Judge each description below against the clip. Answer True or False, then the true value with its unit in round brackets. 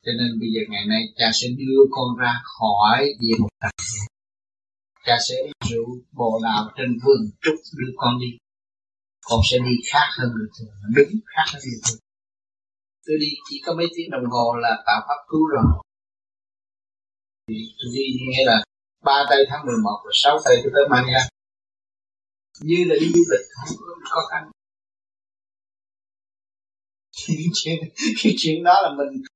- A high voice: False (120 Hz)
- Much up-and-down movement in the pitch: True (6.4 semitones)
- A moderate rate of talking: False (160 wpm)